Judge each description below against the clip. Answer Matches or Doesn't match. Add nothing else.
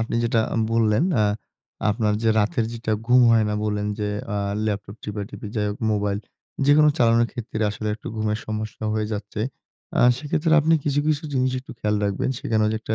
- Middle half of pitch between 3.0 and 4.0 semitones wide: Doesn't match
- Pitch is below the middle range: Matches